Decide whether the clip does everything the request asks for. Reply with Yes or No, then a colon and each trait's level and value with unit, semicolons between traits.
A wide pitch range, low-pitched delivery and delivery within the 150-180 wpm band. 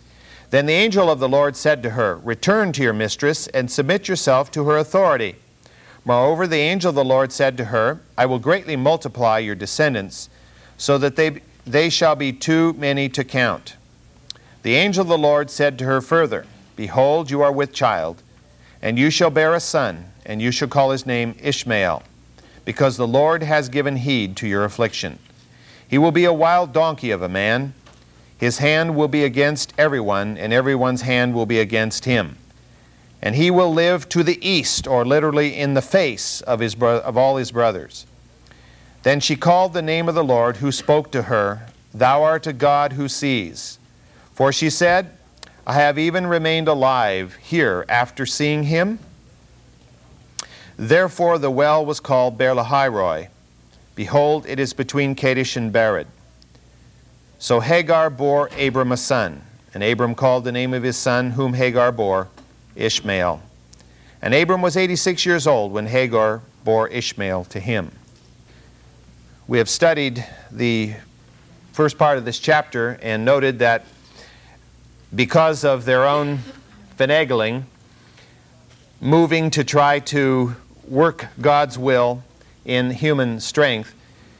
No: average, 4.7 semitones; low, 130 Hz; average, 155 wpm